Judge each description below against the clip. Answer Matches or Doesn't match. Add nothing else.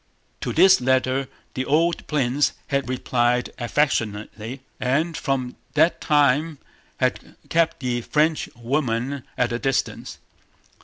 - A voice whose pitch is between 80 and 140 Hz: Matches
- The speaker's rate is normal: Doesn't match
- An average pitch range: Matches